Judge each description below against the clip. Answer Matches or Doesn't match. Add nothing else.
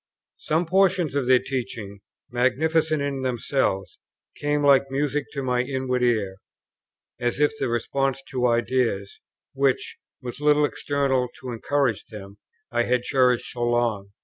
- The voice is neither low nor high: Doesn't match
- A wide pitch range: Doesn't match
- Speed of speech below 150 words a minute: Matches